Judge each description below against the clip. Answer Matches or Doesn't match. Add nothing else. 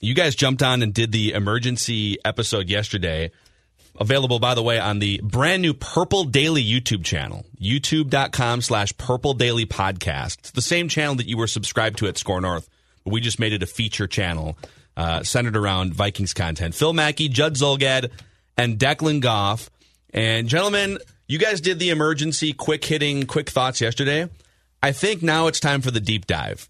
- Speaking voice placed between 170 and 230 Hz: Doesn't match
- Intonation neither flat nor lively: Doesn't match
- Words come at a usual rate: Matches